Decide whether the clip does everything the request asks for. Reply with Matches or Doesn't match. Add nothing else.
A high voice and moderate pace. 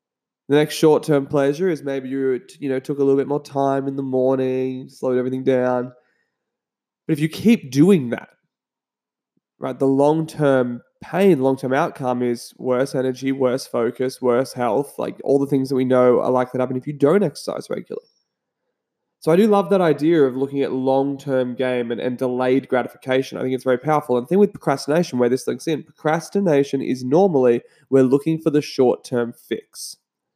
Doesn't match